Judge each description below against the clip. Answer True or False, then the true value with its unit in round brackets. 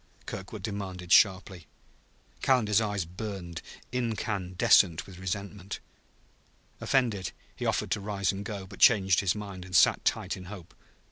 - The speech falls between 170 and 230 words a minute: False (135 wpm)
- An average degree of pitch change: False (2.2 semitones)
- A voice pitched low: True (100 Hz)